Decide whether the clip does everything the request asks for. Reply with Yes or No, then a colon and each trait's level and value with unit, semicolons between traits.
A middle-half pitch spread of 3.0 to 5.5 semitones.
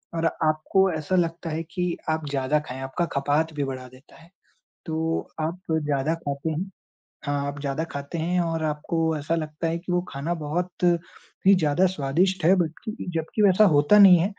Yes: average, 3.3 semitones